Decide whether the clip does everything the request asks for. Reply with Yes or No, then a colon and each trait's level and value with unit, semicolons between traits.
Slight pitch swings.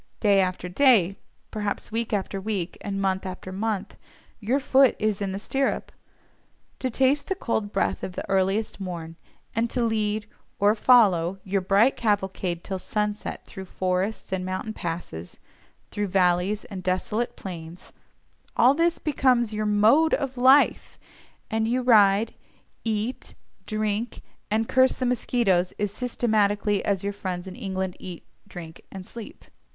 No: average, 3.5 semitones